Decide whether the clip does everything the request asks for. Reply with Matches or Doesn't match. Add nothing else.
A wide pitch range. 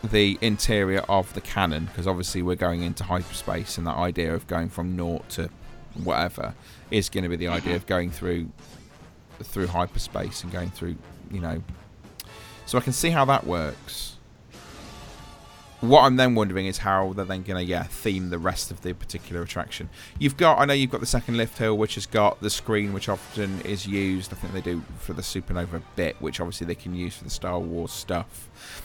Doesn't match